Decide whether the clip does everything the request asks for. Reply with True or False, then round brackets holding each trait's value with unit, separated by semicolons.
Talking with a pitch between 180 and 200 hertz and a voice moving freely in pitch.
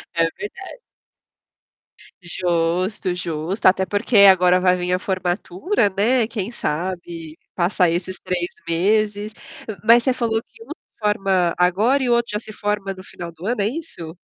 False (190 Hz; 3.5 semitones)